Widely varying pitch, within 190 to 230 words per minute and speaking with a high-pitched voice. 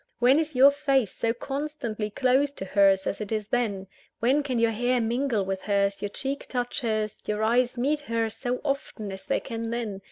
No: average, 4.1 semitones; average, 200 wpm; high, 235 Hz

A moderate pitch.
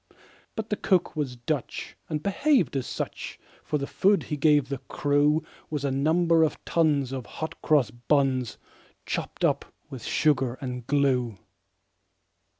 Yes: medium, 145 Hz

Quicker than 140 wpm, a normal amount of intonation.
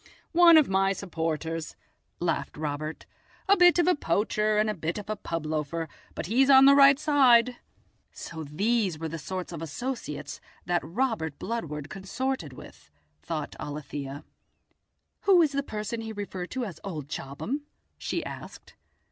No: average, 160 wpm; wide, 8.2 semitones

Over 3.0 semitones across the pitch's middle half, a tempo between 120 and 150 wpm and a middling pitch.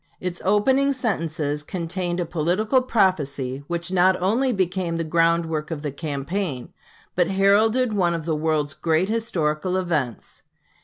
Yes: average, 3.9 semitones; average, 145 wpm; medium, 175 Hz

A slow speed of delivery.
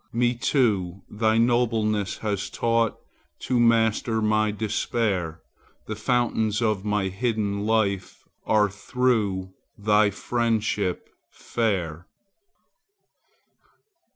Yes: slow, 90 wpm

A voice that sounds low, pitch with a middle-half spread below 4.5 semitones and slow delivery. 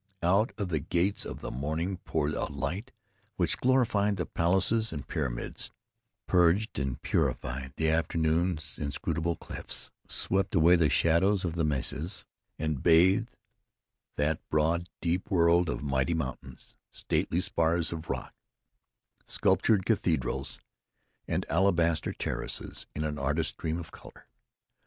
Yes: very low, 85 Hz; average, 3.2 semitones; slow, 130 wpm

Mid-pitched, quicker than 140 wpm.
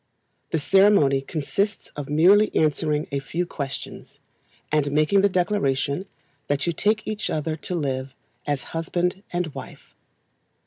No: medium, 155 Hz; slow, 135 wpm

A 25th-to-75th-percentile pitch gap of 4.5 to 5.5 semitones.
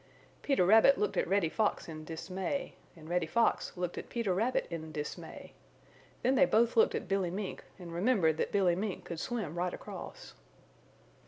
Yes: average, 4.9 semitones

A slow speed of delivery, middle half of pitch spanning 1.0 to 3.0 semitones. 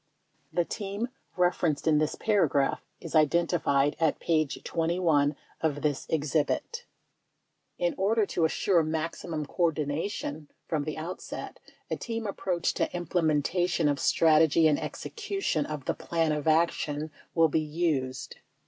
Yes: slow, 130 wpm; narrow, 2.6 semitones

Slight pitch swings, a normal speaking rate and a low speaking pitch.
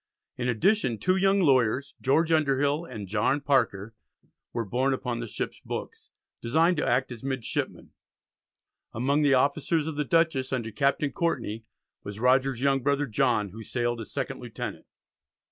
No: average, 3.8 semitones; average, 155 wpm; low, 130 Hz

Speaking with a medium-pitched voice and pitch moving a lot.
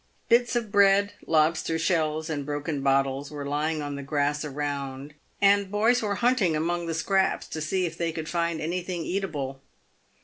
No: medium, 160 Hz; average, 4.7 semitones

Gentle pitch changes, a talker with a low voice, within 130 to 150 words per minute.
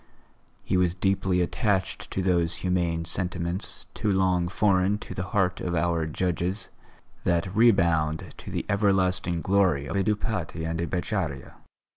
Yes: narrow, 2.1 semitones; very low, 90 Hz; average, 145 wpm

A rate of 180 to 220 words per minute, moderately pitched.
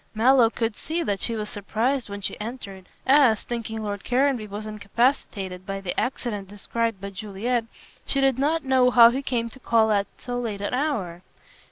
No: average, 185 wpm; high, 225 Hz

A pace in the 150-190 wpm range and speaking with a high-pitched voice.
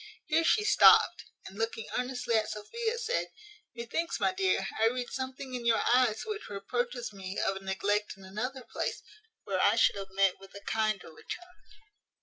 Yes: average, 175 wpm; high, 235 Hz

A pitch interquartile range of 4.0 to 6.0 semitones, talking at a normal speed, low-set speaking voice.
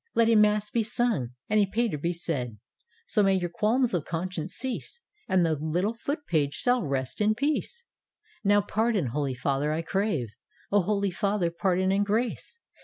No: average, 5.2 semitones; average, 180 wpm; high, 195 Hz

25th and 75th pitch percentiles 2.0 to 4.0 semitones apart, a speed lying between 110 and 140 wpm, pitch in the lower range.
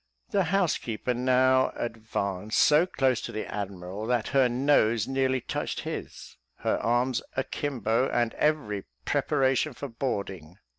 Yes: average, 3.7 semitones; slow, 135 wpm; low, 125 Hz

